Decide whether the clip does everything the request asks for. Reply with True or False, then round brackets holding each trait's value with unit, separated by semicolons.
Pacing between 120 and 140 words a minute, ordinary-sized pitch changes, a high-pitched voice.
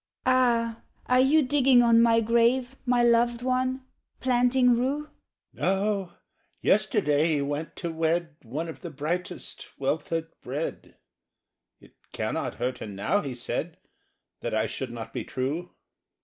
False (135 wpm; 8.7 semitones; 205 Hz)